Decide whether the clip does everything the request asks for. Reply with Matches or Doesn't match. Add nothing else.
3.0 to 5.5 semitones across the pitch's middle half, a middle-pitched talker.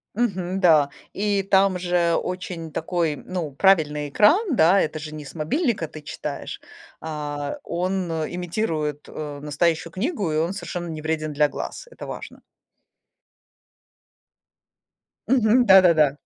Matches